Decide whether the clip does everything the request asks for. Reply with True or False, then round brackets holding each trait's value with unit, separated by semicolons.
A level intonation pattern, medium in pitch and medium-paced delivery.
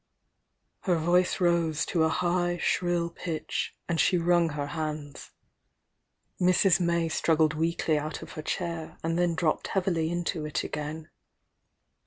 True (1.8 semitones; 170 Hz; 145 wpm)